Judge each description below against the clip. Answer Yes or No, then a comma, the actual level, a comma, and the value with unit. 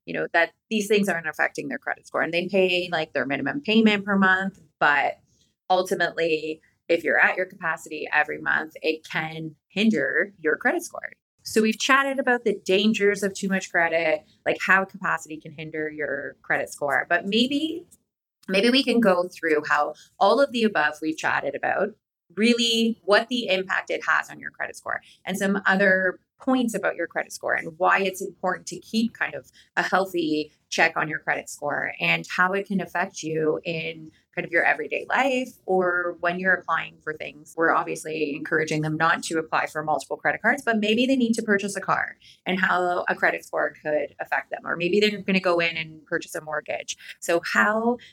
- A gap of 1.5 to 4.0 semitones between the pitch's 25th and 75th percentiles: No, average, 4.5 semitones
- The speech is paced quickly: No, average, 195 wpm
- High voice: No, medium, 180 Hz